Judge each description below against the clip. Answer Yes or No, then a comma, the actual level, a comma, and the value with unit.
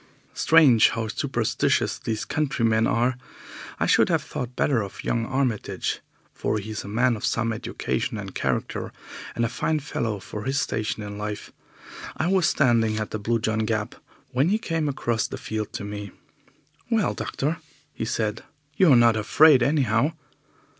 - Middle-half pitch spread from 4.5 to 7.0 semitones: No, average, 4.1 semitones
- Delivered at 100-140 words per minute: No, average, 165 wpm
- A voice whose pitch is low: Yes, low, 115 Hz